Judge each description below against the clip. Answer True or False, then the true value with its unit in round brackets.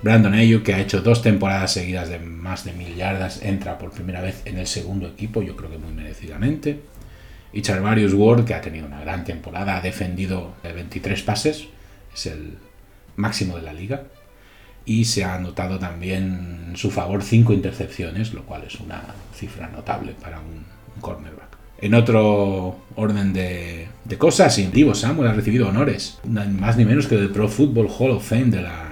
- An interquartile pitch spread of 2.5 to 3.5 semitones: True (3.1 semitones)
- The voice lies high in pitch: False (100 Hz)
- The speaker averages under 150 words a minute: False (180 wpm)